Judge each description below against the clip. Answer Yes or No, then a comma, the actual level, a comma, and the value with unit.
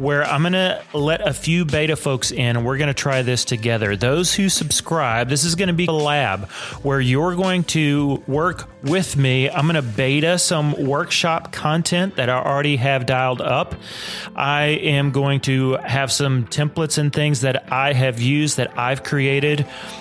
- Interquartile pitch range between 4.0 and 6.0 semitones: No, average, 3.1 semitones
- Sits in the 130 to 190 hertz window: Yes, medium, 140 Hz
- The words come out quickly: No, average, 175 wpm